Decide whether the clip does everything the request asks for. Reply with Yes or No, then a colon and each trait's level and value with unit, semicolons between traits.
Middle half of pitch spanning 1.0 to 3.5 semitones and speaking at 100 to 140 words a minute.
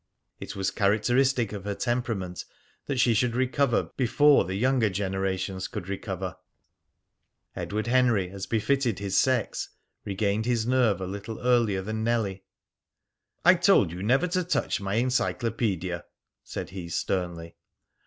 No: average, 4.5 semitones; slow, 135 wpm